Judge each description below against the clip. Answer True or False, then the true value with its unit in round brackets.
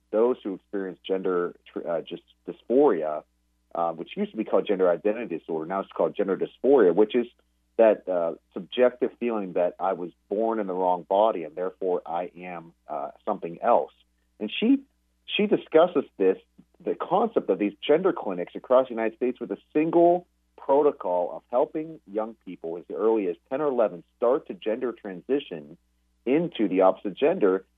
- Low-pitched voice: True (95 Hz)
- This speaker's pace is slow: False (170 wpm)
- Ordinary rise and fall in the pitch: False (5.7 semitones)